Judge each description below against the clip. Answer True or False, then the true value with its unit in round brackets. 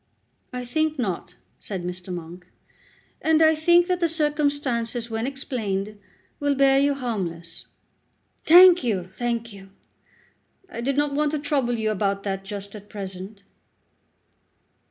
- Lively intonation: True (6.6 semitones)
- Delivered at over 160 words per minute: False (135 wpm)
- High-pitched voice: True (235 Hz)